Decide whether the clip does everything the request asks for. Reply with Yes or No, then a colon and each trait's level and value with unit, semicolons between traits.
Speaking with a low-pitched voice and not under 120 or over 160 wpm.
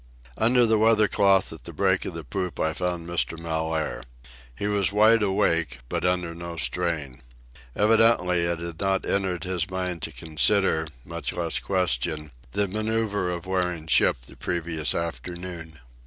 Yes: very low, 90 Hz; average, 155 wpm